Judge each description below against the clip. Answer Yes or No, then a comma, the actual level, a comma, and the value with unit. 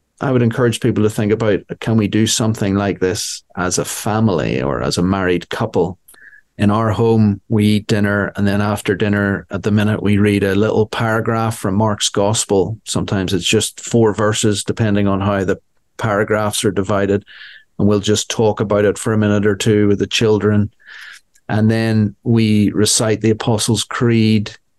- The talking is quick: No, average, 180 wpm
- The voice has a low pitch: Yes, low, 105 Hz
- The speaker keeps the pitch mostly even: Yes, narrow, 1.6 semitones